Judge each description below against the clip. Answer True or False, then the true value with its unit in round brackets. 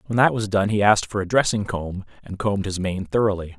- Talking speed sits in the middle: False (250 wpm)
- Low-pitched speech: True (100 Hz)